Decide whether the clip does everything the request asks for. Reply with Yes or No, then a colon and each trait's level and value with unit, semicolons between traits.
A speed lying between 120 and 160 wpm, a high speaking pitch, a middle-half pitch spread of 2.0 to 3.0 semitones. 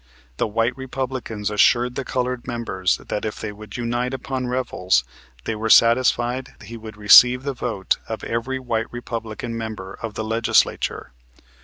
No: average, 155 wpm; low, 115 Hz; narrow, 2.5 semitones